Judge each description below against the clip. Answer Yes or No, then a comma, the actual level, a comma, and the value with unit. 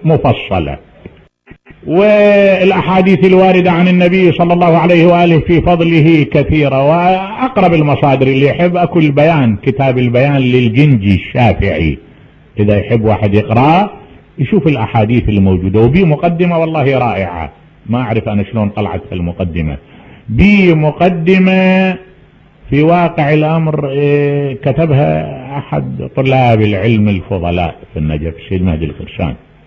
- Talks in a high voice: No, medium, 140 Hz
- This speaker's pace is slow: Yes, slow, 110 wpm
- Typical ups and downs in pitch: No, wide, 8.7 semitones